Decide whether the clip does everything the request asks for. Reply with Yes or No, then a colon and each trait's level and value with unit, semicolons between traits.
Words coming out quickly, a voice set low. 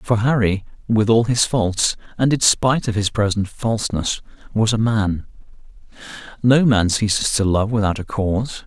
No: average, 165 wpm; low, 110 Hz